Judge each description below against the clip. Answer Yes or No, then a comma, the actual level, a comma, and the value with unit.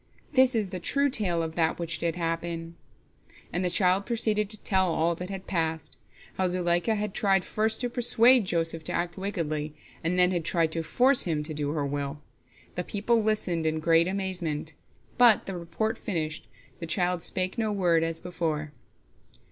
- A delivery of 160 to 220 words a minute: Yes, average, 180 wpm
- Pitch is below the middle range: No, medium, 175 Hz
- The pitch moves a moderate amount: Yes, average, 3.6 semitones